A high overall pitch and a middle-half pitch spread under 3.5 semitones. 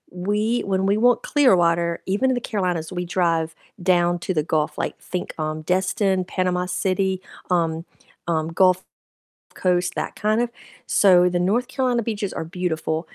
No: medium, 180 Hz; average, 2.8 semitones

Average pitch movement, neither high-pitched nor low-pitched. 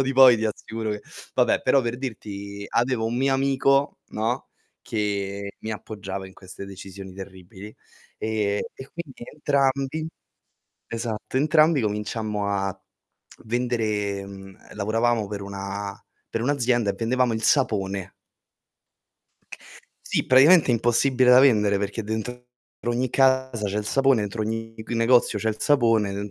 No: average, 4.0 semitones; low, 110 Hz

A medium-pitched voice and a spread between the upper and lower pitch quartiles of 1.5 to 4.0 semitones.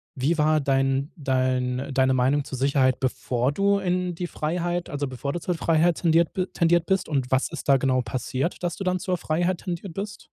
No: medium, 155 Hz; average, 4.9 semitones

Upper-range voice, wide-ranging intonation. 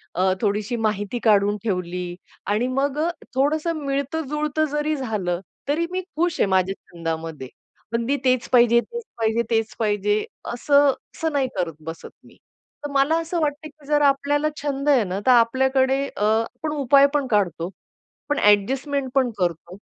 Yes: very high, 255 Hz; wide, 5.9 semitones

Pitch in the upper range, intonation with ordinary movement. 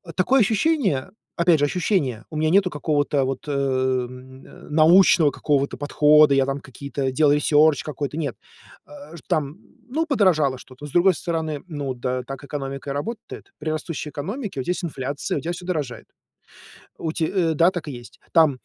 No: medium, 150 Hz; average, 4.1 semitones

